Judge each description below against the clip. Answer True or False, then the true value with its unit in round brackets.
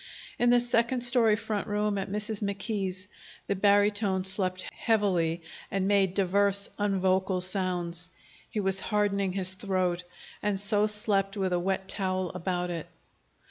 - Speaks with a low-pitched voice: False (195 Hz)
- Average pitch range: False (1.9 semitones)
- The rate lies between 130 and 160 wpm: True (140 wpm)